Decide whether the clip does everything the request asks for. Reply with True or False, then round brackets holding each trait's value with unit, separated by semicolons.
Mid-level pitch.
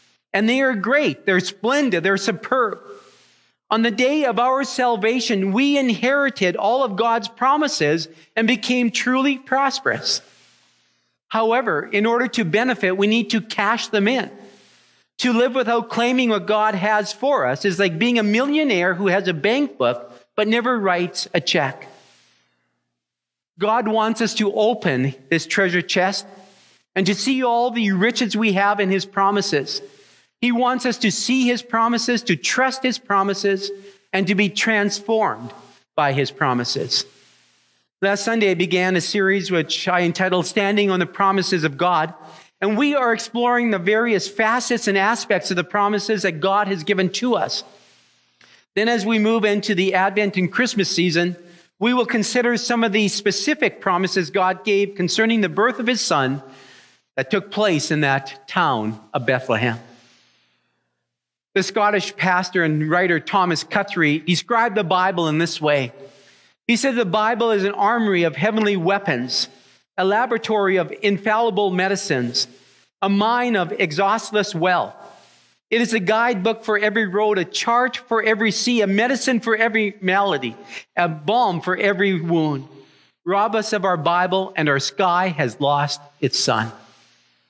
False (200 Hz)